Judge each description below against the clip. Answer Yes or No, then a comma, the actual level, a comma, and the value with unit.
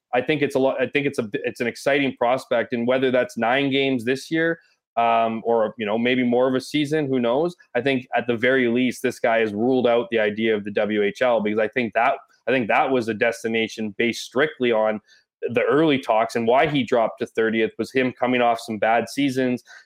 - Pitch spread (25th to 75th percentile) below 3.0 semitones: Yes, narrow, 2.6 semitones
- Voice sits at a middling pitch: No, low, 120 Hz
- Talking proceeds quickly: Yes, fast, 230 wpm